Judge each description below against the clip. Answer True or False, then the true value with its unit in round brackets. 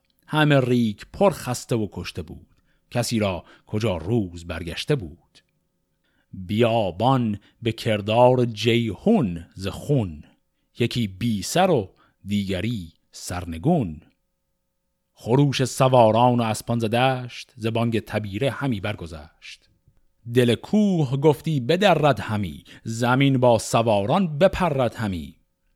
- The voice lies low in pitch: True (115 Hz)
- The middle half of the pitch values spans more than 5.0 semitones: False (4.7 semitones)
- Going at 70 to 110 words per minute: True (105 wpm)